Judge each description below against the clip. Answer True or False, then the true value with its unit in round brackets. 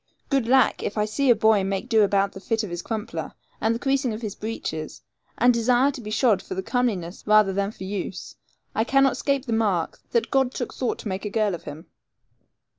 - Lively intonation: False (3.9 semitones)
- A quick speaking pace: True (225 wpm)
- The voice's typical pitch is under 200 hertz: False (220 Hz)